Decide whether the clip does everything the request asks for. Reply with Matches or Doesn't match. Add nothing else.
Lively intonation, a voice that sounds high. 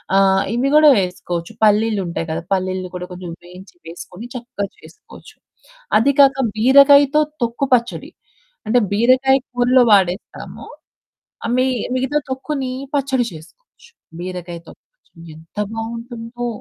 Matches